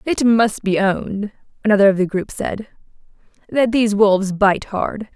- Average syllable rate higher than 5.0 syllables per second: No, 4.9 syllables/s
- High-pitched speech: Yes, high, 210 Hz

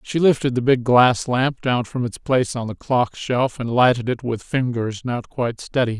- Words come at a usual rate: No, fast, 220 wpm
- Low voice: Yes, low, 125 Hz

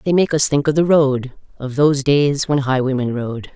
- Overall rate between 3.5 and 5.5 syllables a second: Yes, 5.0 syllables/s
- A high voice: No, medium, 140 Hz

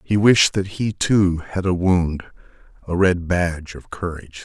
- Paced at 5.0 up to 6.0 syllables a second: No, 4.5 syllables/s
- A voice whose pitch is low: Yes, very low, 90 Hz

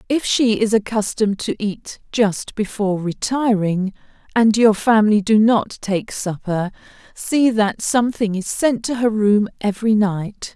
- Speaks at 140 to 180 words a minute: Yes, average, 150 wpm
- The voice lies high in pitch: Yes, high, 215 Hz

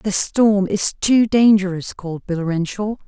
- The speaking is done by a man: No, female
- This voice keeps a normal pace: Yes, average, 155 wpm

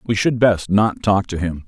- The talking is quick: Yes, fast, 250 wpm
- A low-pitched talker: Yes, low, 100 Hz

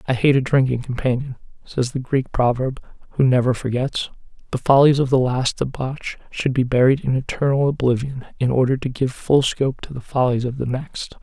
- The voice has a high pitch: No, low, 130 Hz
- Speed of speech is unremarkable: Yes, average, 190 wpm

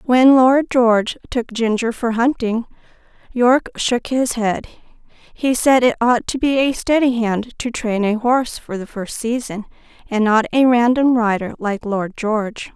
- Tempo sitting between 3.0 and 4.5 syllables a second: Yes, 4.4 syllables/s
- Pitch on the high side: Yes, high, 235 Hz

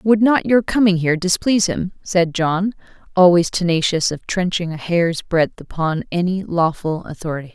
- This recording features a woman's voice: Yes, female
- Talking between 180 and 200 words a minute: No, average, 160 wpm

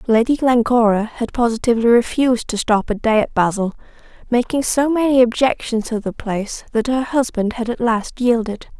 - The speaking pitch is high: Yes, high, 235 Hz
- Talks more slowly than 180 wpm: Yes, average, 170 wpm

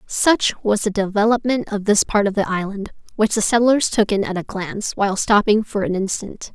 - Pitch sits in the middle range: No, high, 210 Hz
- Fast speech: Yes, fast, 210 wpm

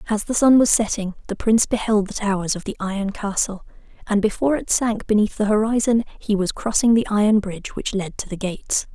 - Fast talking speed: Yes, fast, 215 wpm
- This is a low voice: No, high, 210 Hz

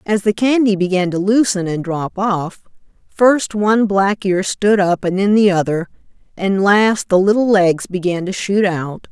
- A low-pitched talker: No, high, 195 Hz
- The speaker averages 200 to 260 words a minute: No, average, 185 wpm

